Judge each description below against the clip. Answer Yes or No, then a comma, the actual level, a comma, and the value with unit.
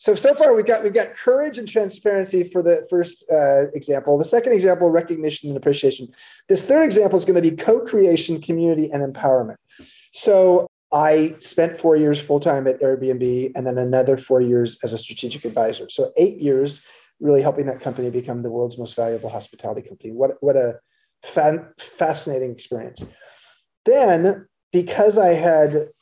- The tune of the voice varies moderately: No, wide, 6.2 semitones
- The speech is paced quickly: No, average, 170 wpm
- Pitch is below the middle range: No, medium, 155 Hz